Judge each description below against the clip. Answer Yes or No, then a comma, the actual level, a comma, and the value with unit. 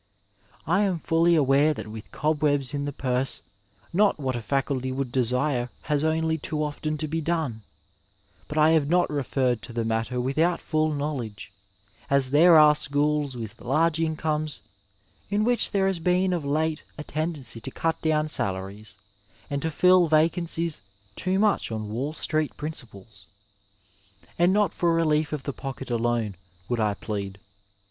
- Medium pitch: Yes, medium, 150 Hz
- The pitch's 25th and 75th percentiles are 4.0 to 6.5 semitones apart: Yes, average, 4.3 semitones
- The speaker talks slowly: No, average, 160 wpm